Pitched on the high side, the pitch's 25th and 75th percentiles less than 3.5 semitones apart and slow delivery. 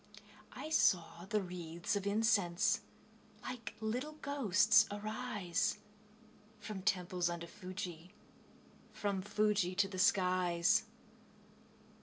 Yes: high, 195 Hz; average, 3.0 semitones; slow, 95 wpm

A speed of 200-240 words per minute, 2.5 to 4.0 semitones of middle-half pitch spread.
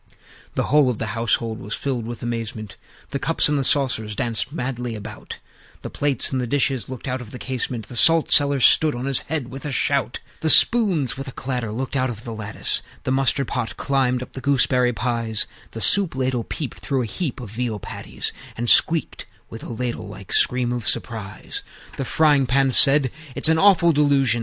Yes: fast, 205 wpm; average, 3.2 semitones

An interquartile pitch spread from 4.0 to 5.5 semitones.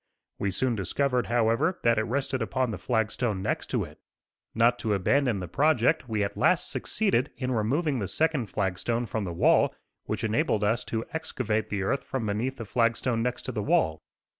No: average, 3.6 semitones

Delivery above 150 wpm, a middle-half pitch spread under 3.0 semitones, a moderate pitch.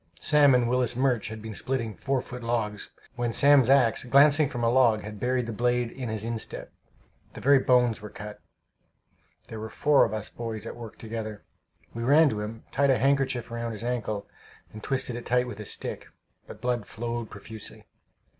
No: average, 190 wpm; narrow, 2.6 semitones; low, 120 Hz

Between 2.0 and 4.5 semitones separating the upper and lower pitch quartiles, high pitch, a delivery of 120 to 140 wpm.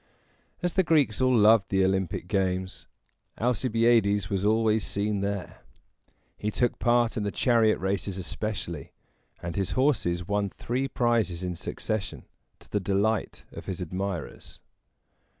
No: average, 3.4 semitones; low, 105 Hz; slow, 135 wpm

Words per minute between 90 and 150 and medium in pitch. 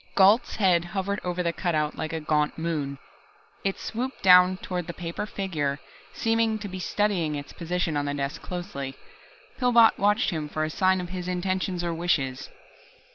No: average, 175 wpm; medium, 180 Hz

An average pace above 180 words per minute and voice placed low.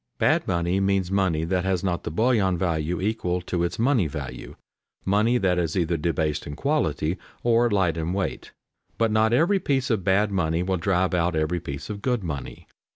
Yes: average, 190 wpm; very low, 95 Hz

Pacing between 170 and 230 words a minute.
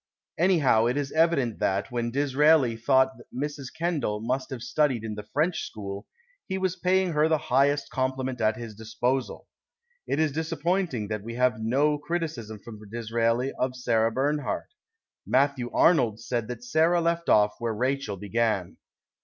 No: average, 155 wpm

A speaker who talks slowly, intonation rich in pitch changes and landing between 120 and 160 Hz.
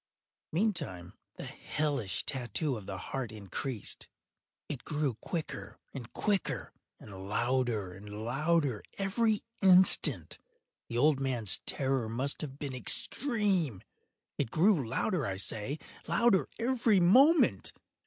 Yes: slow, 115 wpm; wide, 8.5 semitones; low, 135 Hz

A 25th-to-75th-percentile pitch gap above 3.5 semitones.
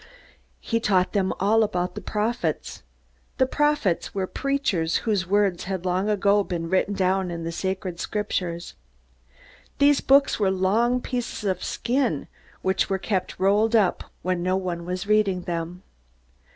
No: average, 3.0 semitones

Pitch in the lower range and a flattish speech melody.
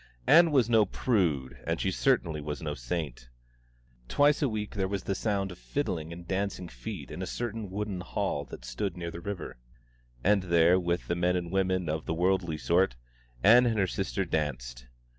No: very low, 90 Hz; average, 3.9 semitones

